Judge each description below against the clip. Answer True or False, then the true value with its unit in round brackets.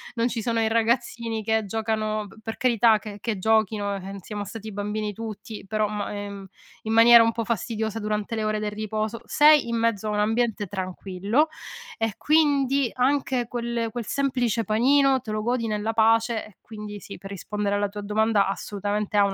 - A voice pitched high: True (220 Hz)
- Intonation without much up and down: True (1.9 semitones)